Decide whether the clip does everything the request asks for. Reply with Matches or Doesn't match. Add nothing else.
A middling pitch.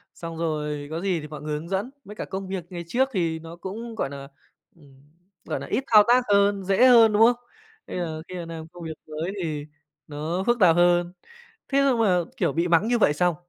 Matches